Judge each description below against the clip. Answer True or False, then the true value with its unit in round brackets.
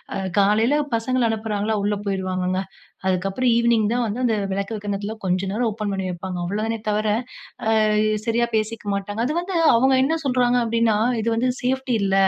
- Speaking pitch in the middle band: False (220 Hz)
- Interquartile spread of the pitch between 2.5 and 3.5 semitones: True (3.1 semitones)